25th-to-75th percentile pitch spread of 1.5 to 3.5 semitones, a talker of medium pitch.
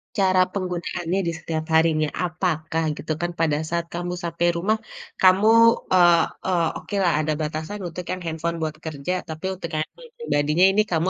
Yes: narrow, 2.5 semitones; medium, 170 Hz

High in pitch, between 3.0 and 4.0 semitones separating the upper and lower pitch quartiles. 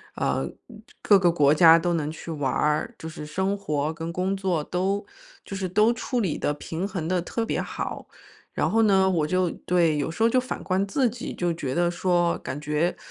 No: medium, 175 Hz; average, 3.7 semitones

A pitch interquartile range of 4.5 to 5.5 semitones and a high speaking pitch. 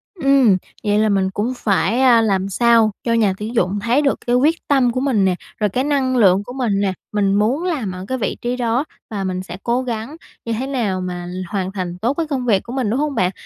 Yes: average, 4.8 semitones; high, 225 Hz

